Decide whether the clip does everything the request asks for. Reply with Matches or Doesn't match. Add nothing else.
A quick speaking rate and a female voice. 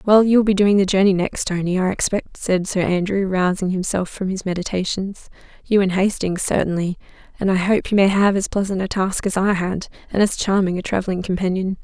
Matches